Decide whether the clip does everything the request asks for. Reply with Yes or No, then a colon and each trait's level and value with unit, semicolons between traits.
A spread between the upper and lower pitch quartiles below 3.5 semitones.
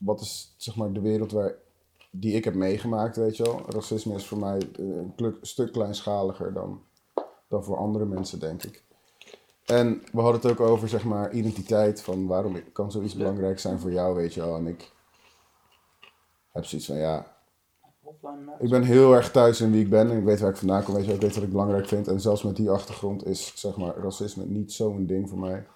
Yes: narrow, 2.6 semitones